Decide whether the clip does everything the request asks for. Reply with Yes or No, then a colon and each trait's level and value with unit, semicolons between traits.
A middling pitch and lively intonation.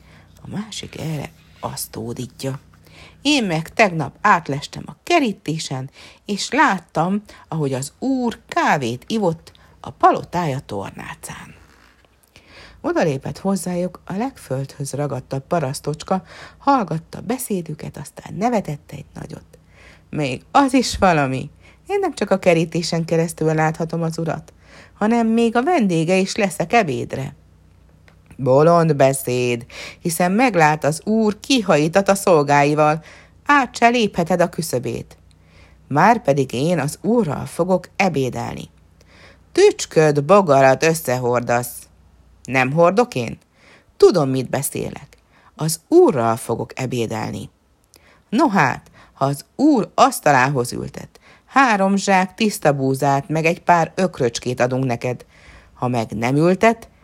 Yes: medium, 155 Hz; wide, 7.3 semitones